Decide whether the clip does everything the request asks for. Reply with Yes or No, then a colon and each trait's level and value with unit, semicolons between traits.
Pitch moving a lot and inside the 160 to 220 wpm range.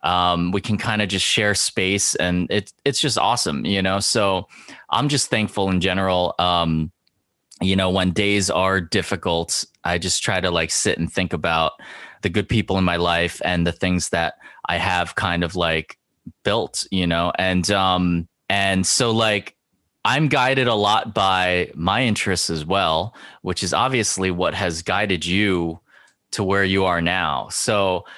No: average, 2.7 semitones; average, 175 wpm